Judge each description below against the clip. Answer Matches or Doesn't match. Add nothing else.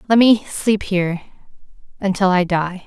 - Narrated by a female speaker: Matches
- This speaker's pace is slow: Matches